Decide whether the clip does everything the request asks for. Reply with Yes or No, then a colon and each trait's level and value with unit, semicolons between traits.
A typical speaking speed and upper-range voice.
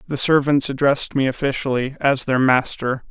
No: average, 155 wpm; low, 135 Hz